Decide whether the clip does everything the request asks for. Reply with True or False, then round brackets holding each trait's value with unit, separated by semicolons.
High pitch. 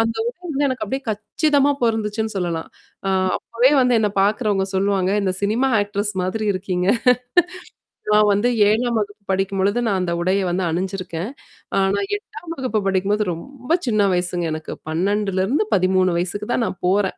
True (205 Hz)